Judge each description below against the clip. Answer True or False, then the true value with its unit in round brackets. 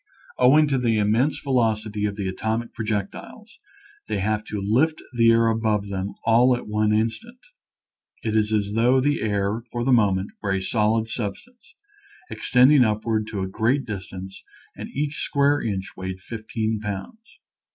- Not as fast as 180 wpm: True (160 wpm)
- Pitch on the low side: True (110 Hz)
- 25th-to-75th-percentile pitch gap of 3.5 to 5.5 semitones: False (3.0 semitones)